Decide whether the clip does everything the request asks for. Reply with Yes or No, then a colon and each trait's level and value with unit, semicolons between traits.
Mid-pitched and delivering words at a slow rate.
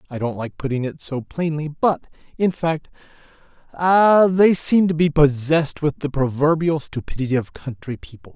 No: medium, 150 Hz; average, 165 wpm